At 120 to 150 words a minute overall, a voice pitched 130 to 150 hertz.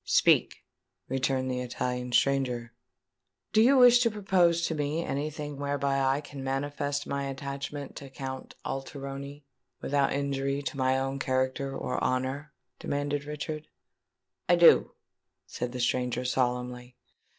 Yes: slow, 135 wpm; medium, 140 Hz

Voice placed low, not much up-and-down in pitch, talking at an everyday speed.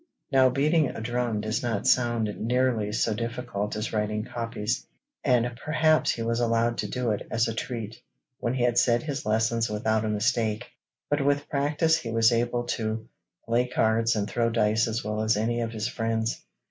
Yes: low, 115 Hz; narrow, 1.9 semitones; average, 185 wpm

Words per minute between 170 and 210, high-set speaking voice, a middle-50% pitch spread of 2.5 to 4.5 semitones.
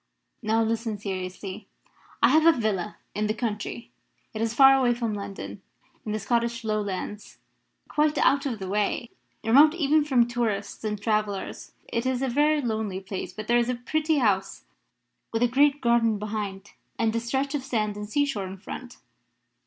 Yes: average, 175 wpm; high, 225 Hz; average, 3.5 semitones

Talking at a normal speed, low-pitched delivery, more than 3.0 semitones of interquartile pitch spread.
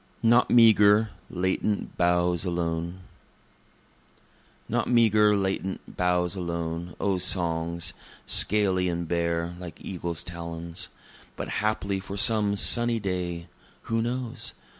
No: slow, 105 wpm; very low, 90 Hz; average, 3.5 semitones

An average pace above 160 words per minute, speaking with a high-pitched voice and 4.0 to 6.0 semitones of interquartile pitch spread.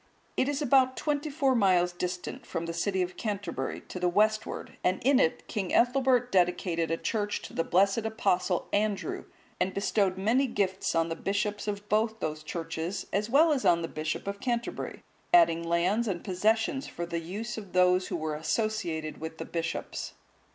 Yes: average, 180 wpm; high, 195 Hz; average, 4.6 semitones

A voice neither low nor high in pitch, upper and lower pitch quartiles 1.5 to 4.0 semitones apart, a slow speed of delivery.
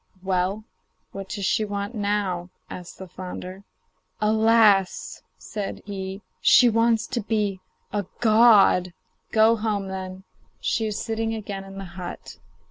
No: high, 200 Hz; narrow, 2.5 semitones; slow, 130 wpm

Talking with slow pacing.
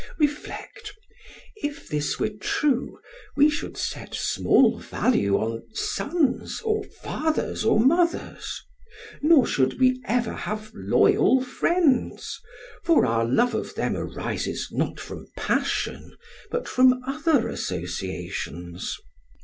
Yes: slow, 110 wpm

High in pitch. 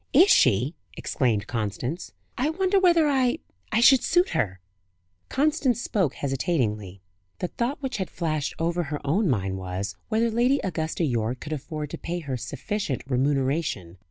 No: medium, 155 Hz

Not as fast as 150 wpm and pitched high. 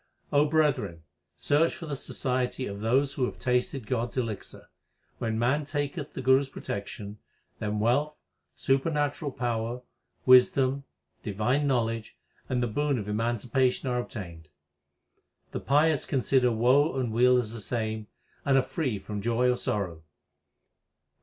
No: average, 140 wpm; low, 125 Hz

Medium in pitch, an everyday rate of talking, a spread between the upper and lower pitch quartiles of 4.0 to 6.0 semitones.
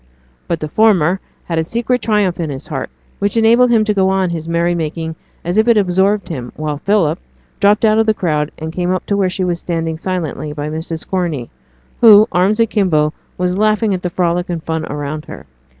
No: medium, 180 Hz; fast, 215 wpm; average, 4.3 semitones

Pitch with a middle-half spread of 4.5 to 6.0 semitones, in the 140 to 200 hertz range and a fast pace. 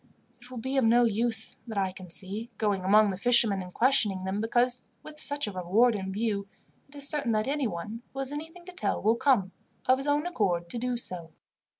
No: average, 5.0 semitones; high, 230 Hz; fast, 220 wpm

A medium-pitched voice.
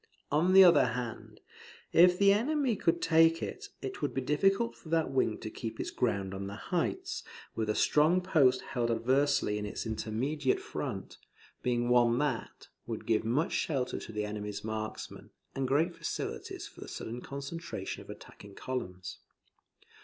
No: low, 130 Hz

